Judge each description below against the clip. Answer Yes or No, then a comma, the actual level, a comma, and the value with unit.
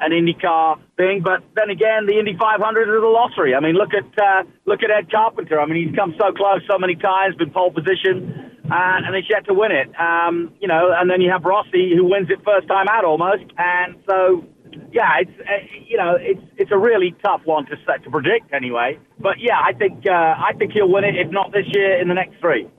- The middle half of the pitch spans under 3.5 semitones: Yes, average, 2.8 semitones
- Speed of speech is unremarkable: No, fast, 240 wpm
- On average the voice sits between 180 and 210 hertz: Yes, high, 190 Hz